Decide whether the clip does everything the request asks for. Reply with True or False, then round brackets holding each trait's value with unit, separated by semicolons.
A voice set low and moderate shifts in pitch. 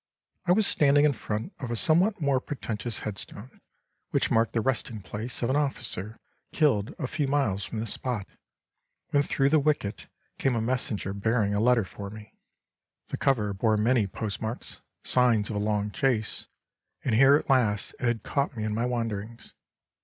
True (115 Hz; 4.1 semitones)